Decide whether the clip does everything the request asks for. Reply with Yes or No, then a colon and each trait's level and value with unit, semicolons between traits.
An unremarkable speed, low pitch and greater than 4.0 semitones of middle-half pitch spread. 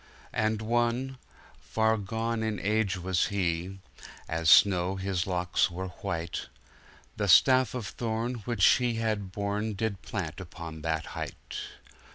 No: average, 150 wpm; low, 100 Hz; average, 3.7 semitones